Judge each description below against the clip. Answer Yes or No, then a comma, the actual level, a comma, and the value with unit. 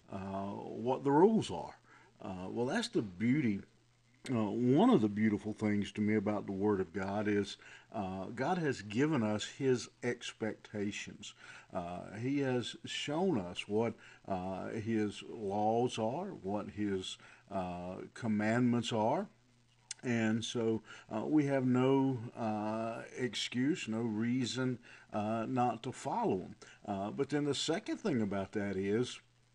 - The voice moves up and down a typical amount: Yes, average, 3.1 semitones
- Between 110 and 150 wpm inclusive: Yes, average, 140 wpm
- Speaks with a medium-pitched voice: No, low, 110 Hz